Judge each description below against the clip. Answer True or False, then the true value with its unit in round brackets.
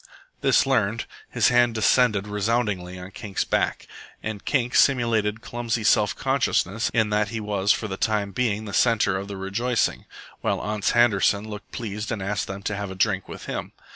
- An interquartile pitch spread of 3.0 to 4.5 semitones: False (2.6 semitones)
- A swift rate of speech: False (180 wpm)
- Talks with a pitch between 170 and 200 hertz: False (105 Hz)